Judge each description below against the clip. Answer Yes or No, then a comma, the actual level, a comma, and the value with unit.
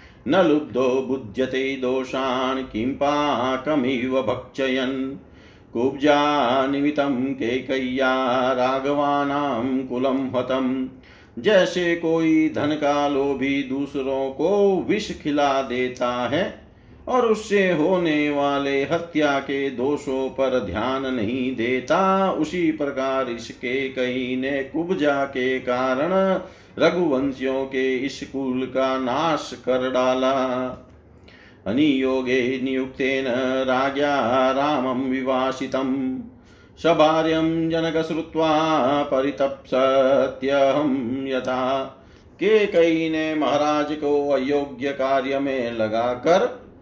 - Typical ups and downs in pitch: No, narrow, 2.0 semitones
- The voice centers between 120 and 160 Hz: Yes, low, 135 Hz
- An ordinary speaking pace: No, slow, 90 wpm